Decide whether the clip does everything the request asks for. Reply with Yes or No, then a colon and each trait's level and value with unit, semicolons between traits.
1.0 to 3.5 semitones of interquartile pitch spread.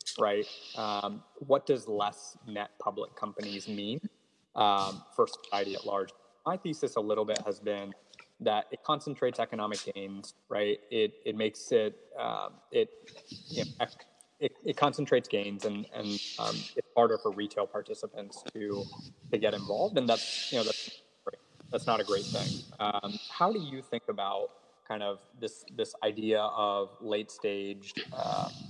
No: average, 4.1 semitones